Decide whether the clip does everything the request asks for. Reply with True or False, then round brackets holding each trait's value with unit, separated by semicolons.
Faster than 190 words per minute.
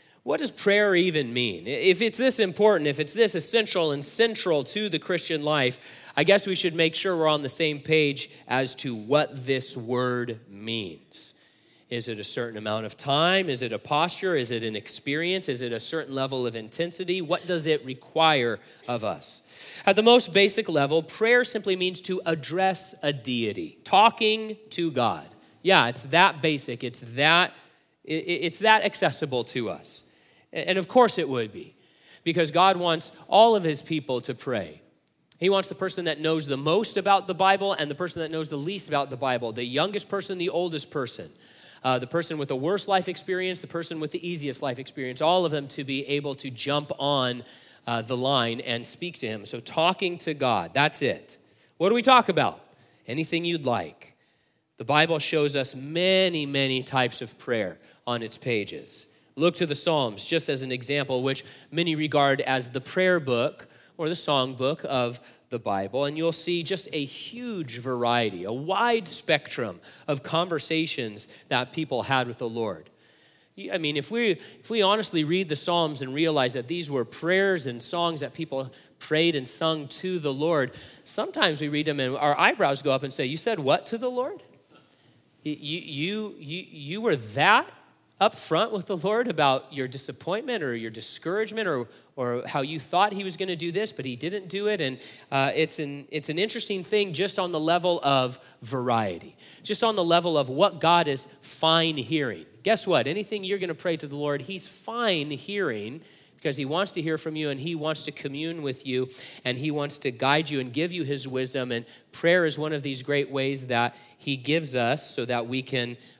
True (200 wpm)